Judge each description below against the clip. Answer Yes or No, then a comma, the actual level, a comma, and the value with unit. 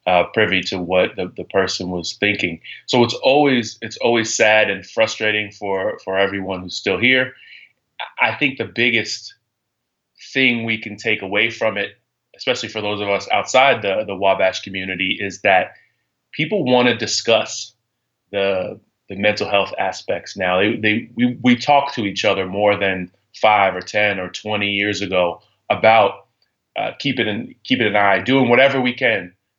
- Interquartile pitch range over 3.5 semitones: No, average, 3.2 semitones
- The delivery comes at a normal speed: Yes, average, 170 wpm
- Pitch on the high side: No, low, 105 Hz